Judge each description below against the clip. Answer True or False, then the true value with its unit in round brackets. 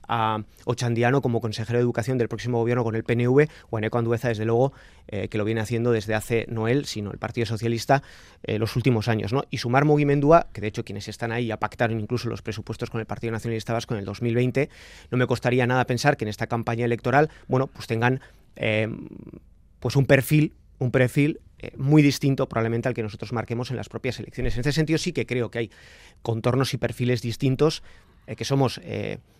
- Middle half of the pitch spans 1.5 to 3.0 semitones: True (2.5 semitones)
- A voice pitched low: True (120 Hz)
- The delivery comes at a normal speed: False (215 wpm)